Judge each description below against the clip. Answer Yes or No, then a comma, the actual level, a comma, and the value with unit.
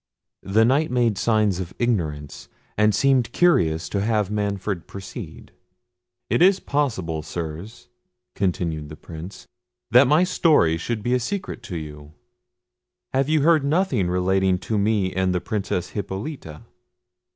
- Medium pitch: No, low, 100 Hz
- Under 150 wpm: Yes, average, 140 wpm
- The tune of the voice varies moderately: No, wide, 6.1 semitones